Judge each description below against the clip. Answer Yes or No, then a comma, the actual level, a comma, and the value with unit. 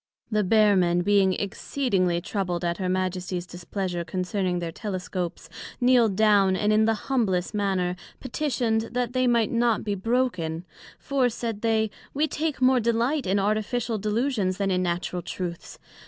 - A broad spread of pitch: No, average, 4.3 semitones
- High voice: Yes, high, 205 Hz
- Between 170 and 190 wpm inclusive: No, average, 155 wpm